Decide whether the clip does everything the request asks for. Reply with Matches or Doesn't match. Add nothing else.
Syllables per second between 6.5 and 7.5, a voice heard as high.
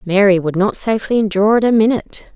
Matches